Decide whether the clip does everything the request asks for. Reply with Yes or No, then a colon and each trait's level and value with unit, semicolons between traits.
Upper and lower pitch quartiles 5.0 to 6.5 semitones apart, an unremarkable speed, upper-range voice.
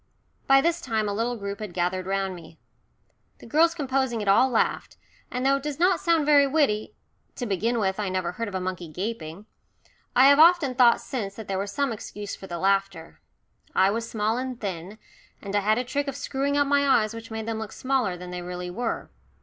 No: wide, 5.6 semitones; fast, 220 wpm; high, 220 Hz